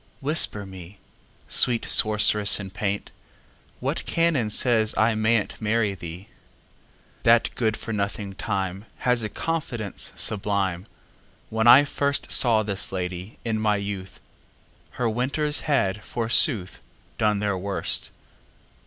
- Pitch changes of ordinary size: Yes, average, 3.0 semitones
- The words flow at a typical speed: No, slow, 95 wpm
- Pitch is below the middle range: Yes, low, 105 Hz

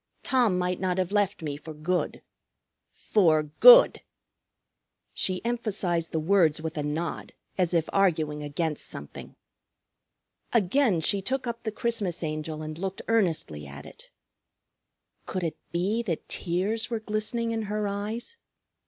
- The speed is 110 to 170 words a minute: Yes, average, 140 wpm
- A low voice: No, medium, 185 Hz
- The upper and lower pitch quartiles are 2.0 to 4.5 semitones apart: No, average, 5.2 semitones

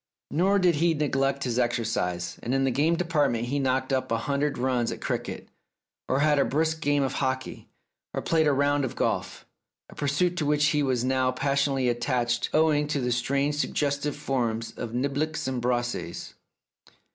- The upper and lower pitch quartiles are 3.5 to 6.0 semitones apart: No, average, 3.0 semitones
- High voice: No, low, 135 Hz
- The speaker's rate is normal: Yes, average, 180 wpm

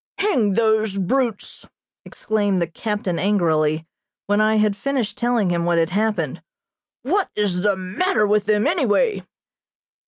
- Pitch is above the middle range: Yes, high, 210 Hz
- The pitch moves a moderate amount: Yes, average, 3.2 semitones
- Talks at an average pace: Yes, average, 145 wpm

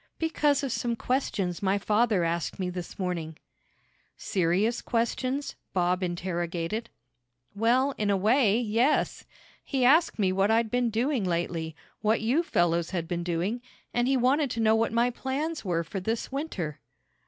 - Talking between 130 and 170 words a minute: Yes, average, 155 wpm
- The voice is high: Yes, high, 215 Hz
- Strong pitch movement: Yes, wide, 5.7 semitones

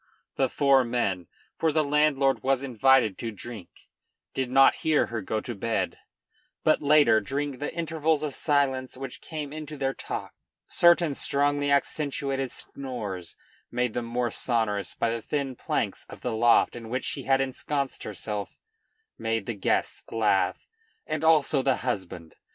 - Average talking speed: Yes, average, 155 wpm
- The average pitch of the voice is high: No, low, 135 Hz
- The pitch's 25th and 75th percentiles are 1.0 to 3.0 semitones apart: No, average, 3.8 semitones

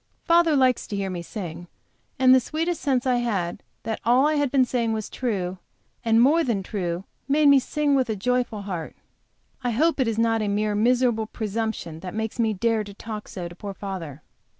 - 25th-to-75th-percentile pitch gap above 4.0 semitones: Yes, average, 4.5 semitones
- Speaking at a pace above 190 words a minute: Yes, average, 200 wpm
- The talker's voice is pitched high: Yes, high, 225 Hz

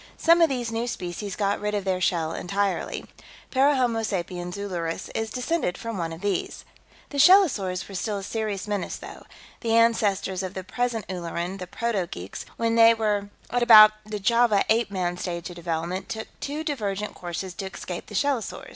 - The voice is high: Yes, high, 205 Hz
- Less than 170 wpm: No, average, 180 wpm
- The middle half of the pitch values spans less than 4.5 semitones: Yes, average, 3.9 semitones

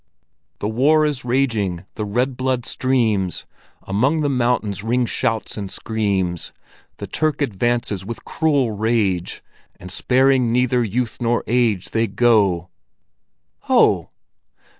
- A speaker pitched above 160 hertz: No, low, 115 Hz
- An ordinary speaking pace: No, slow, 120 wpm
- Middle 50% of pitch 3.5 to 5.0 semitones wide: Yes, average, 3.8 semitones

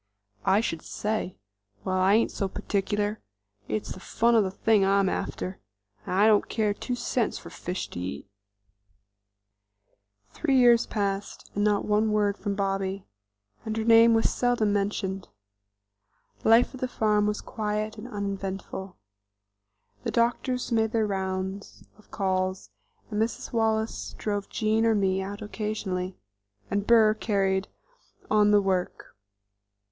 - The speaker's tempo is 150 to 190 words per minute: No, average, 140 wpm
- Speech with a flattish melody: Yes, narrow, 2.3 semitones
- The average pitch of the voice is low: No, high, 205 Hz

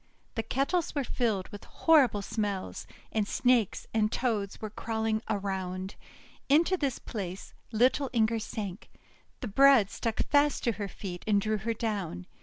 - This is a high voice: Yes, high, 220 Hz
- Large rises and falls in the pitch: No, average, 3.8 semitones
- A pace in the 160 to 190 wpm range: No, average, 150 wpm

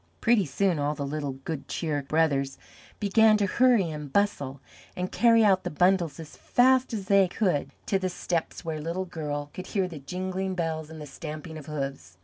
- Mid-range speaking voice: Yes, medium, 165 Hz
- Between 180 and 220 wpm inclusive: Yes, average, 190 wpm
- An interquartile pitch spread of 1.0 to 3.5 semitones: No, average, 4.6 semitones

